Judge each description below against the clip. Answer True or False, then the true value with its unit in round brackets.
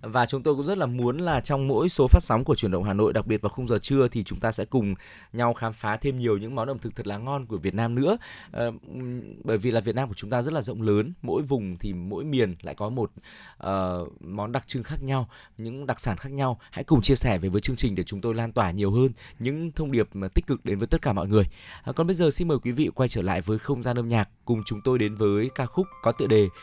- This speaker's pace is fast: True (285 wpm)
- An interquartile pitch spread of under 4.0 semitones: False (4.3 semitones)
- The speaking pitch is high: False (115 Hz)